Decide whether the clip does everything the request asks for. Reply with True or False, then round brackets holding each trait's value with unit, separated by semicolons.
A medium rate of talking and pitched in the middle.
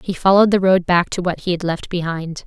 False (270 wpm; 180 Hz)